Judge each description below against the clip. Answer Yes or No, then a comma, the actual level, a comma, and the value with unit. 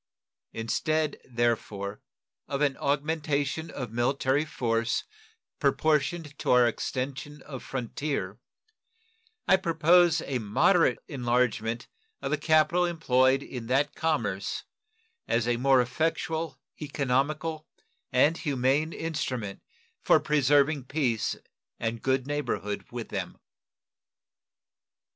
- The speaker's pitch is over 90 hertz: Yes, medium, 140 Hz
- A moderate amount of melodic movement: Yes, average, 4.1 semitones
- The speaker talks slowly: Yes, slow, 100 wpm